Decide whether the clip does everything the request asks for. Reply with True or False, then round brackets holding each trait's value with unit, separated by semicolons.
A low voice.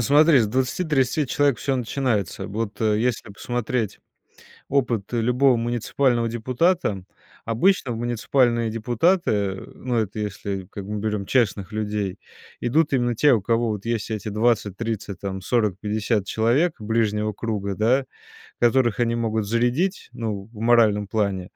True (115 Hz)